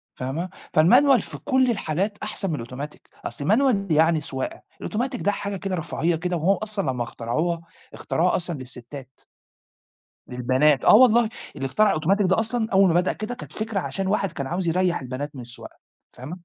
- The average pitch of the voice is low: No, medium, 175 Hz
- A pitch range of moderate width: No, wide, 6.6 semitones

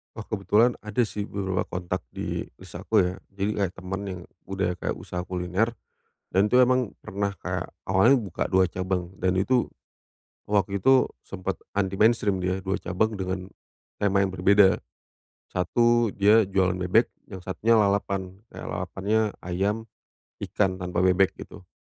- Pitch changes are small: Yes, narrow, 2.3 semitones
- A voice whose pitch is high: No, very low, 95 Hz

